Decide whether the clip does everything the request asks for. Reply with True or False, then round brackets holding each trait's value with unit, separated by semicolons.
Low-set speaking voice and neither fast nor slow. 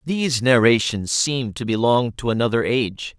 True (120 Hz; 150 wpm)